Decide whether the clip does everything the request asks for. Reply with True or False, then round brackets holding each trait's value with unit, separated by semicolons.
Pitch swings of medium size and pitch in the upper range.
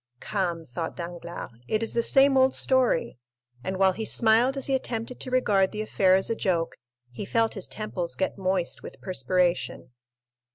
True (4.7 semitones; 195 Hz)